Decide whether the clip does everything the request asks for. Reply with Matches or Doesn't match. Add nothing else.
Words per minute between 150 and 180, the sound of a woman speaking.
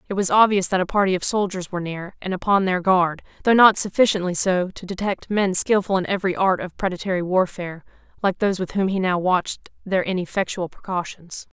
Doesn't match